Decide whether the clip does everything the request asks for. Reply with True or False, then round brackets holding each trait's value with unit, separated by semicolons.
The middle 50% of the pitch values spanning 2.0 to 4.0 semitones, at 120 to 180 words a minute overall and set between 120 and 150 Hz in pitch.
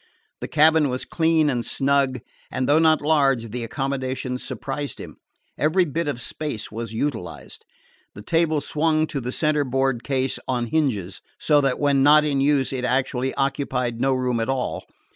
True (2.9 semitones; 165 wpm; 135 Hz)